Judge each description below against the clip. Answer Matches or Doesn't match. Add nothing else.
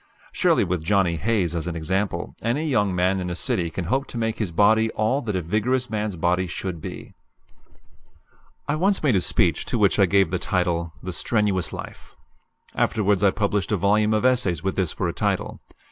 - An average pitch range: Matches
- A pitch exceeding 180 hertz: Doesn't match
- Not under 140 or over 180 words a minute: Doesn't match